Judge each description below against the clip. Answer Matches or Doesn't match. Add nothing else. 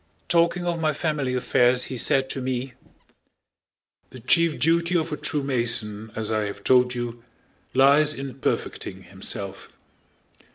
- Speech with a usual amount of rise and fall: Matches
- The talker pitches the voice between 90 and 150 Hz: Matches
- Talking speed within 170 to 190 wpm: Doesn't match